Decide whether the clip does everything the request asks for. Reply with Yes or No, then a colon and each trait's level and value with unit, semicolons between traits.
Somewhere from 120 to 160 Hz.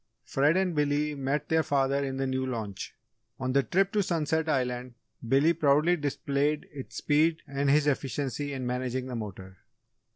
Yes: medium, 140 Hz